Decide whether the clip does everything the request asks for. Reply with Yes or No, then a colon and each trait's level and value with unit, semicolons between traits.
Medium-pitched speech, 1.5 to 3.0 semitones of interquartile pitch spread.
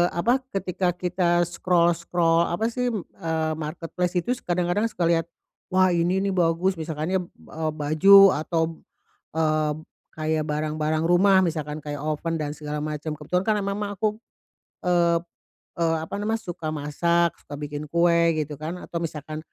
Yes: medium, 170 Hz; narrow, 2.6 semitones